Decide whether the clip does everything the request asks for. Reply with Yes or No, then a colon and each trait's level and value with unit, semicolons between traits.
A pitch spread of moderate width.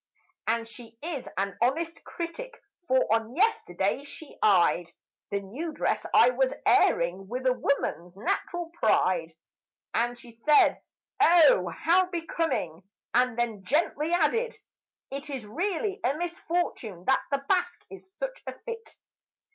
No: wide, 8.0 semitones